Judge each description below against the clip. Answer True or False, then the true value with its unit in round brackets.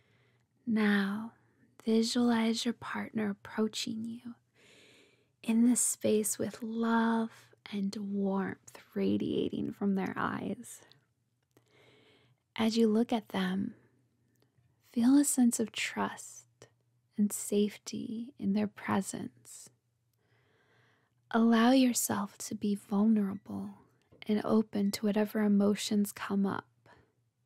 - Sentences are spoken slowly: True (95 wpm)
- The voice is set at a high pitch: True (205 Hz)